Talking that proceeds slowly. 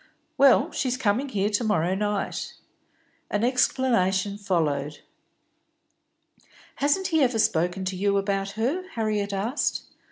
Yes: slow, 120 wpm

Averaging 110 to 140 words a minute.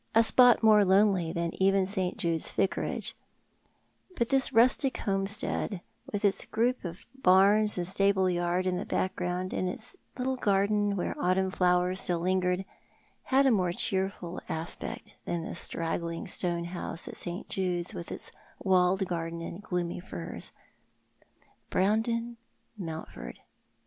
Yes: slow, 135 wpm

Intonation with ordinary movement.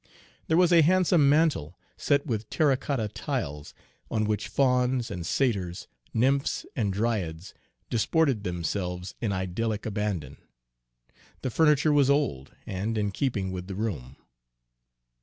No: wide, 6.8 semitones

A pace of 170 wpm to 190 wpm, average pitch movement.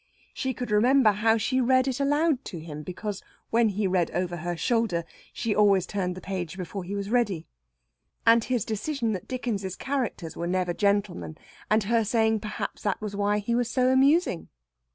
Yes: average, 185 wpm; average, 4.6 semitones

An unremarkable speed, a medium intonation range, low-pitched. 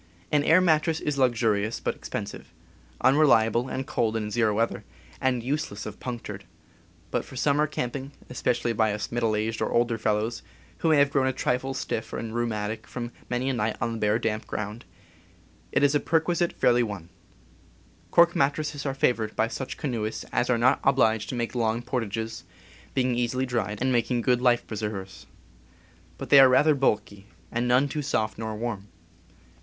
Yes: average, 180 wpm; average, 3.3 semitones; low, 120 Hz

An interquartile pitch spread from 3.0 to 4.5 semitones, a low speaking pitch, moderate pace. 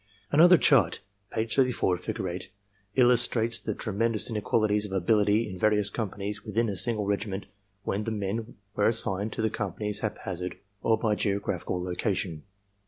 No: narrow, 2.6 semitones; low, 105 Hz; average, 160 wpm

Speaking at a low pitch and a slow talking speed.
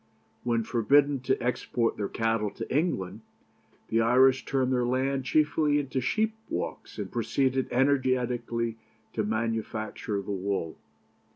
Yes: low, 125 Hz; slow, 125 wpm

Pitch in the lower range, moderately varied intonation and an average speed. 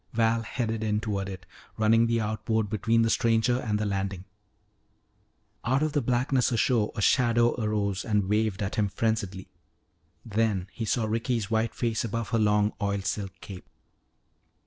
No: low, 110 Hz; narrow, 2.1 semitones; average, 160 wpm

